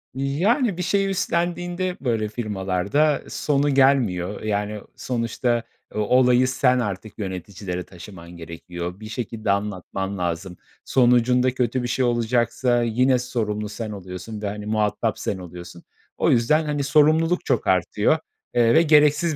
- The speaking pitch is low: Yes, low, 115 Hz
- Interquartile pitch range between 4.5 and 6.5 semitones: Yes, average, 5.3 semitones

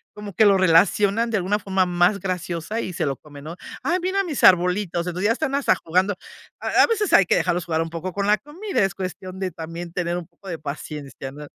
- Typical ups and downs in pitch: Yes, average, 3.7 semitones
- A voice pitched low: No, medium, 185 Hz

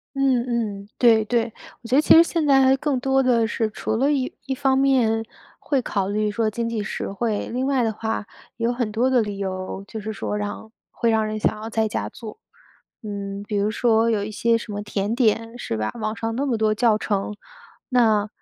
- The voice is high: Yes, high, 225 Hz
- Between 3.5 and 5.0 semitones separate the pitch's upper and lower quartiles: No, average, 2.8 semitones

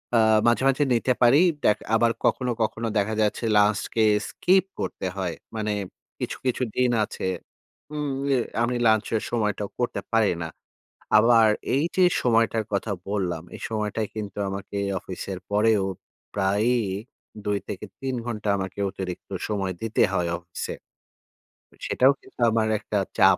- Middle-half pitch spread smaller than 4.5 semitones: Yes, average, 2.8 semitones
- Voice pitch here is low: Yes, low, 110 Hz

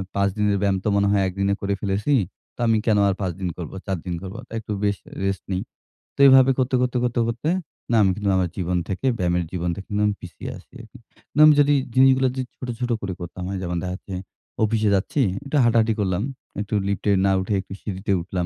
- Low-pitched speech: Yes, low, 100 Hz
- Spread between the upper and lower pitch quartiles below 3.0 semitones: No, average, 3.7 semitones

